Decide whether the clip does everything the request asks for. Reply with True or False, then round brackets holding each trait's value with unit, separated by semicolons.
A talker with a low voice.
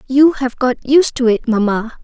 False (255 Hz)